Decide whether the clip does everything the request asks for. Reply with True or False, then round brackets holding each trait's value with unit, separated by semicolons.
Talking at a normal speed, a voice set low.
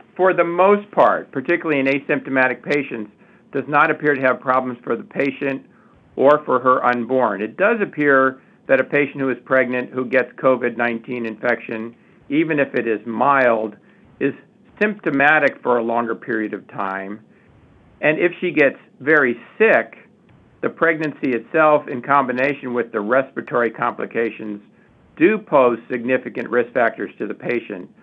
True (150 wpm; 130 Hz)